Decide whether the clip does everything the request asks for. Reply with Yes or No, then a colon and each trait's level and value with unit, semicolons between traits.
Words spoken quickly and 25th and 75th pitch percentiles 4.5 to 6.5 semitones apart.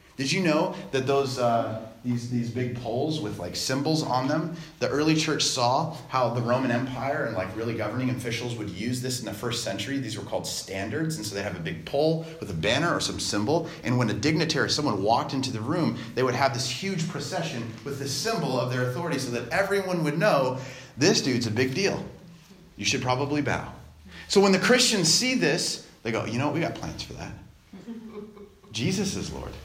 Yes: fast, 215 wpm; average, 5.2 semitones